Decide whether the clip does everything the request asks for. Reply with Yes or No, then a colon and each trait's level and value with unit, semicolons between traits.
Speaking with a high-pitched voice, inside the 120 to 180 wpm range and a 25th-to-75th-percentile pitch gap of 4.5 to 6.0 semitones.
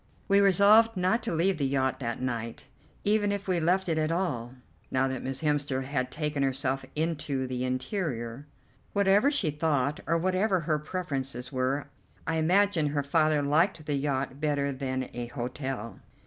No: medium, 150 Hz; average, 165 wpm; average, 5.2 semitones